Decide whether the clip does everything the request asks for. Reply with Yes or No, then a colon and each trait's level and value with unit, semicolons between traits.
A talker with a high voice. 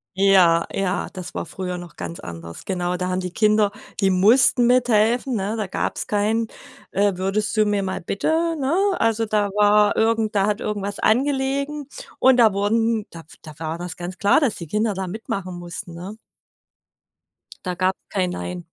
Yes: high, 200 Hz